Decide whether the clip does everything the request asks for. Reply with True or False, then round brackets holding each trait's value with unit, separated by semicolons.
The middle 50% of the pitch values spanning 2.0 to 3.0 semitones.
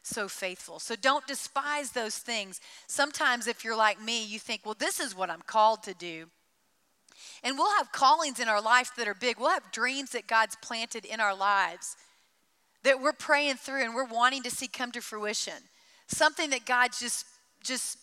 False (3.6 semitones)